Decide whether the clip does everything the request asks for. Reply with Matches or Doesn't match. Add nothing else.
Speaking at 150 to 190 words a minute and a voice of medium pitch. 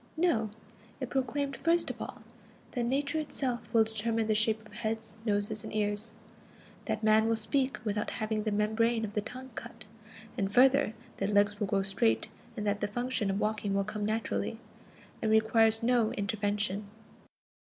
Doesn't match